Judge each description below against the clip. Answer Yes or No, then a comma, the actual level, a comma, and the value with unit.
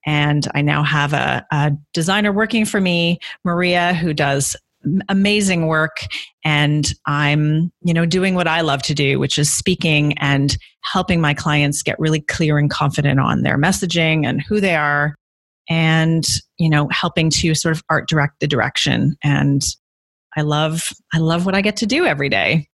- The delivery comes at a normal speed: Yes, average, 175 wpm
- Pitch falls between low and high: Yes, medium, 155 Hz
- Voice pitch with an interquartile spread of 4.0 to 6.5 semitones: No, average, 3.0 semitones